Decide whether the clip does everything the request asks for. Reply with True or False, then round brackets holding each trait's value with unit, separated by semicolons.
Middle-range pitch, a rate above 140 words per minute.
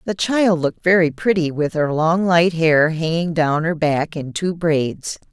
True (165 Hz; 190 wpm)